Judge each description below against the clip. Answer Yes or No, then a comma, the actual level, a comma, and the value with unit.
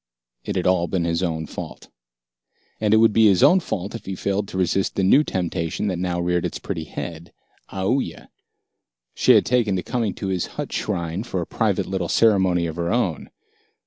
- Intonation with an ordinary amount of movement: Yes, average, 3.2 semitones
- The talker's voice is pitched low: Yes, very low, 95 Hz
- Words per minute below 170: No, average, 200 wpm